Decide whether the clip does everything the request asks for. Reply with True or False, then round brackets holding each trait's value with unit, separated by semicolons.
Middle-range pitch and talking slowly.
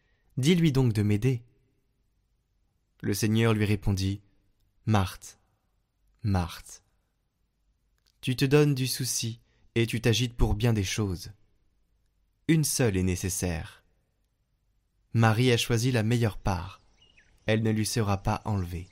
False (105 Hz; 125 wpm)